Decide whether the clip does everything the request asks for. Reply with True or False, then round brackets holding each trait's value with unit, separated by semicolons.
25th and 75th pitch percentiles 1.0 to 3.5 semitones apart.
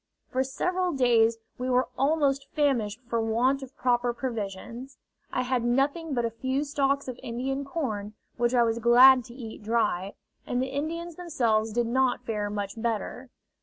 True (2.9 semitones)